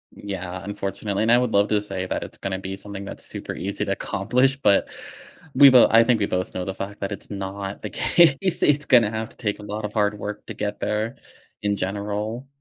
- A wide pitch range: No, narrow, 2.4 semitones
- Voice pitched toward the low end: Yes, low, 105 Hz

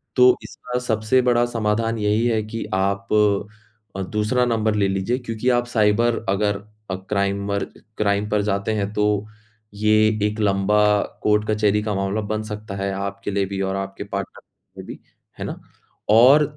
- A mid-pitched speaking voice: No, low, 105 Hz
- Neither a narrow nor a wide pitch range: No, narrow, 2.0 semitones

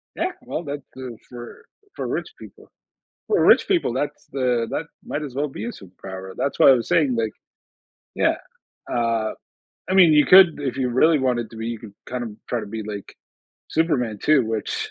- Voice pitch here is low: Yes, low, 125 Hz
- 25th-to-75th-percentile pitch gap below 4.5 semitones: No, average, 4.8 semitones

